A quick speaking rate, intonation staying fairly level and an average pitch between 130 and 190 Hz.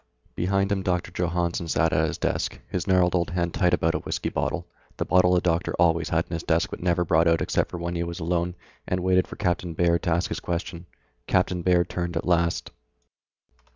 No: fast, 215 wpm; narrow, 1.2 semitones; very low, 85 Hz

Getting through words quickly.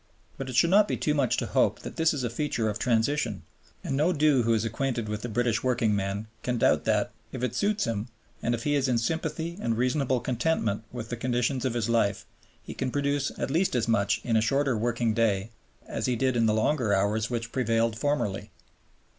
Yes: fast, 220 wpm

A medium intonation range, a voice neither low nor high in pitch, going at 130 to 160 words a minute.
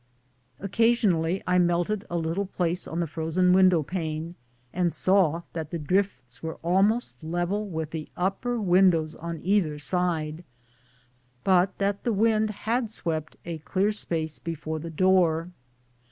Yes: average, 3.3 semitones; medium, 175 Hz; average, 140 wpm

